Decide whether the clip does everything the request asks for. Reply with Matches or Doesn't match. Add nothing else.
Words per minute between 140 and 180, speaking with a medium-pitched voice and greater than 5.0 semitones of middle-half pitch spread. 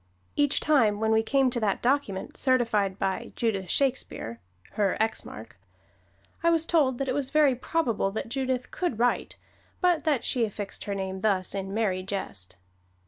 Doesn't match